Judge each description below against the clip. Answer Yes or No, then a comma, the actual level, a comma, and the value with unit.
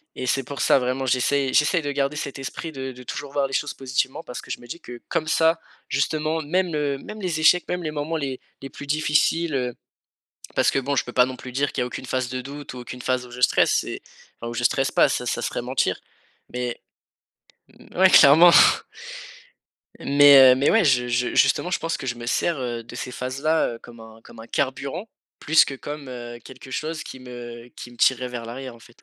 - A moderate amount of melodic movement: Yes, average, 3.2 semitones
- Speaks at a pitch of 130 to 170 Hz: Yes, low, 135 Hz